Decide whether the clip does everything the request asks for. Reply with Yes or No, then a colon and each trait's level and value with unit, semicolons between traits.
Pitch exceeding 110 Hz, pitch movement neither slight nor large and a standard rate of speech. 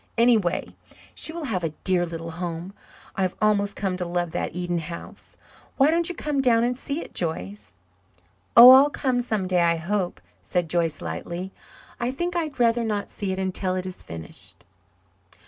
No: high, 190 Hz; wide, 6.0 semitones; average, 180 wpm